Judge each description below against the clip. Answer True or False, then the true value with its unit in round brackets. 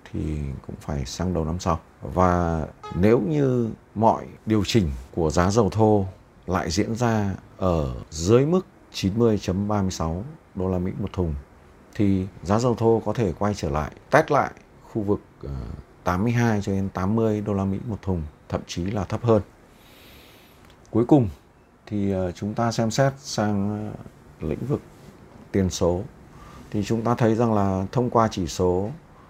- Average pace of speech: False (160 wpm)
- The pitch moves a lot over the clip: False (3.8 semitones)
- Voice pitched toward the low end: True (100 Hz)